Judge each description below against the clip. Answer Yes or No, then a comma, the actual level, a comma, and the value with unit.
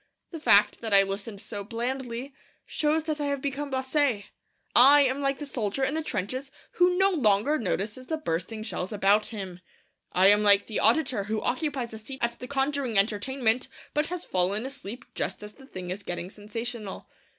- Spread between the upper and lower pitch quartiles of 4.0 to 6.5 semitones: Yes, average, 5.2 semitones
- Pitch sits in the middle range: No, high, 235 Hz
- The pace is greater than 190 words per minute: No, average, 185 wpm